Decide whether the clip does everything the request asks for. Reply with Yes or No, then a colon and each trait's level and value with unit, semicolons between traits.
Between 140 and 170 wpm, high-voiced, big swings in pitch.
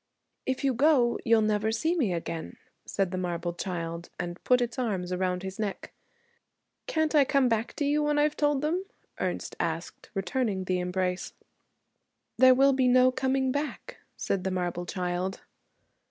Yes: average, 165 wpm; high, 220 Hz; wide, 6.7 semitones